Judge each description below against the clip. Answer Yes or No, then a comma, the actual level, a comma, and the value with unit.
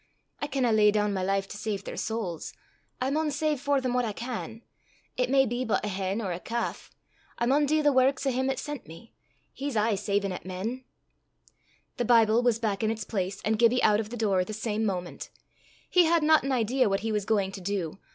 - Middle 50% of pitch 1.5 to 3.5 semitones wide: No, average, 4.3 semitones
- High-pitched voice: Yes, high, 225 Hz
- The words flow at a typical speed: No, fast, 230 wpm